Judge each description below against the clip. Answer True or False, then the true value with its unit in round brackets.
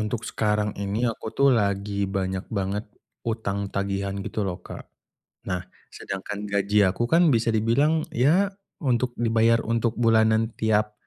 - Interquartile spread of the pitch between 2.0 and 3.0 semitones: True (2.6 semitones)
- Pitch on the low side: True (110 Hz)